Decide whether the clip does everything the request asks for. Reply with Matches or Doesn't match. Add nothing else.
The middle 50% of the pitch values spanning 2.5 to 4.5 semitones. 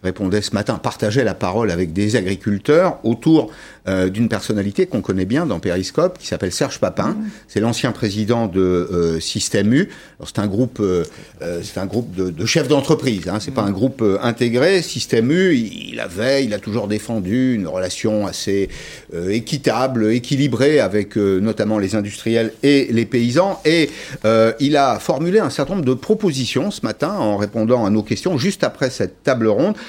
Doesn't match